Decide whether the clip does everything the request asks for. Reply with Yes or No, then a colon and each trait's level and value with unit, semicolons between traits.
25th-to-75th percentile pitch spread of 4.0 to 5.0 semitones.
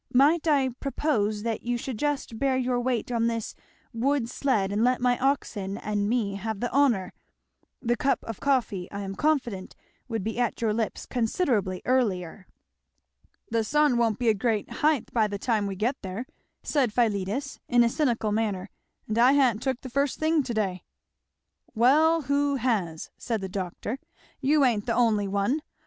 Yes: average, 4.3 semitones